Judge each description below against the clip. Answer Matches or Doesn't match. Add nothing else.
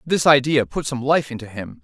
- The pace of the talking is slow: Doesn't match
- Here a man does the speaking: Matches